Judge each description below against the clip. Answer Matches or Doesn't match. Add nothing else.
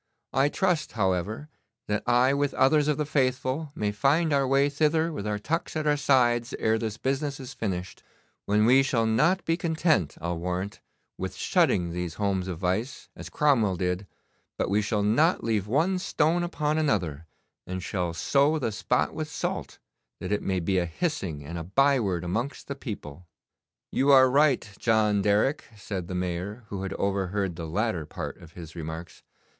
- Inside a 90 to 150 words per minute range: Doesn't match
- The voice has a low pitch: Matches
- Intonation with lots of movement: Matches